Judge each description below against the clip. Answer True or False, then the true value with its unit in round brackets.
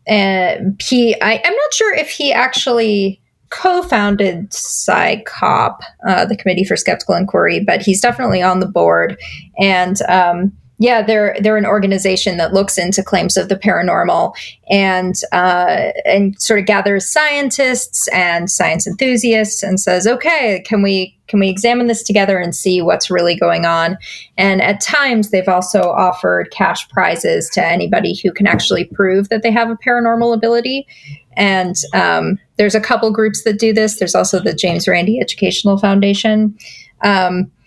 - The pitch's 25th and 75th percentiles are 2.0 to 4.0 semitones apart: True (3.5 semitones)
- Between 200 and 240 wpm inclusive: False (165 wpm)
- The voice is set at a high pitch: True (200 Hz)